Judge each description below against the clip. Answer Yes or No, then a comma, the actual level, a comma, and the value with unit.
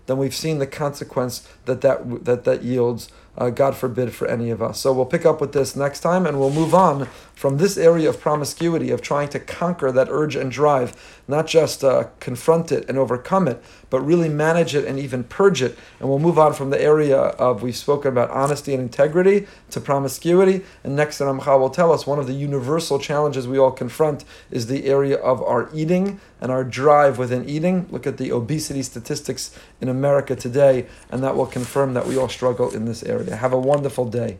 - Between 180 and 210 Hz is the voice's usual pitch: No, medium, 140 Hz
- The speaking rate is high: Yes, fast, 215 wpm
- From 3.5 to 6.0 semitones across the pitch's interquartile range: No, average, 2.9 semitones